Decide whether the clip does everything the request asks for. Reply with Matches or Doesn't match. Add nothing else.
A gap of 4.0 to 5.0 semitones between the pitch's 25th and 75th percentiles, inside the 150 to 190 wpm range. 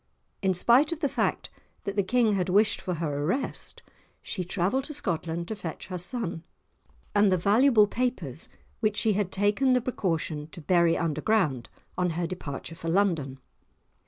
Matches